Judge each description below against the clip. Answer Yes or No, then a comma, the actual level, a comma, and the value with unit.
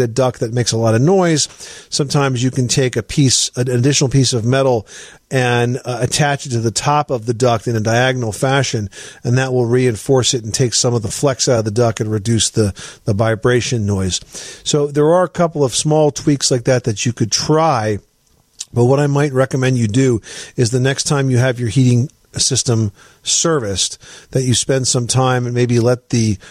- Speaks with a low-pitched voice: Yes, low, 125 Hz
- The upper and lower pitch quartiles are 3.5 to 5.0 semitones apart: No, narrow, 2.6 semitones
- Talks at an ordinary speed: No, fast, 215 wpm